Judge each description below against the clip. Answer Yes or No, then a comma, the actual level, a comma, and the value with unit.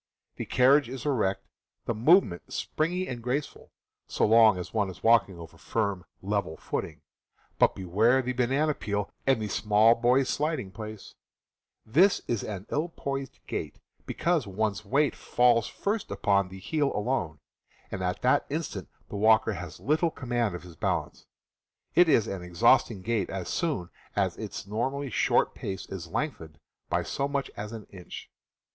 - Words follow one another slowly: No, average, 165 wpm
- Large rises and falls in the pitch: Yes, wide, 5.9 semitones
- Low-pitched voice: Yes, low, 115 Hz